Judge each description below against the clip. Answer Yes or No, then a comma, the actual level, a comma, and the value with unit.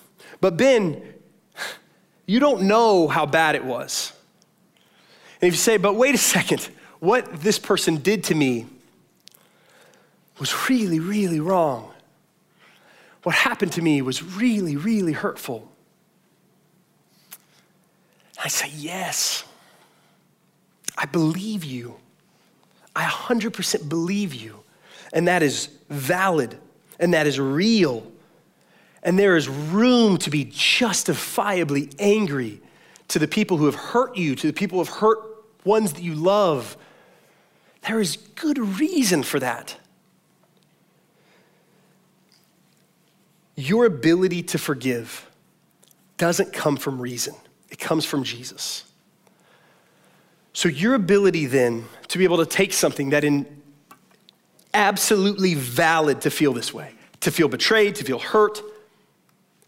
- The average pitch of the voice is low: No, medium, 180 Hz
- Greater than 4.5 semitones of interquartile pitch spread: Yes, average, 5.0 semitones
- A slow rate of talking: Yes, slow, 120 wpm